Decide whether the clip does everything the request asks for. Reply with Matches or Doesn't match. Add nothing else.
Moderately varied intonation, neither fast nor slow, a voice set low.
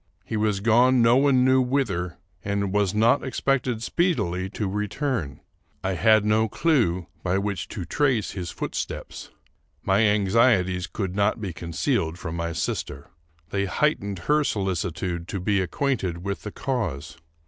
Matches